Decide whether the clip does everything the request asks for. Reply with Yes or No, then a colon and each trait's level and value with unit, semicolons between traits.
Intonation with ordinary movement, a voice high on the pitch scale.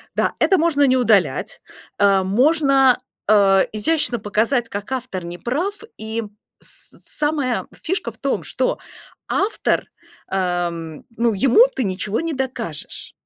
No: wide, 6.2 semitones; high, 235 Hz